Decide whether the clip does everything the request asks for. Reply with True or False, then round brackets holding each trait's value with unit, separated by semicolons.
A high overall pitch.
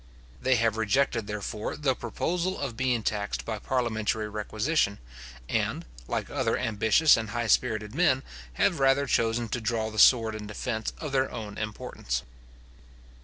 False (115 Hz)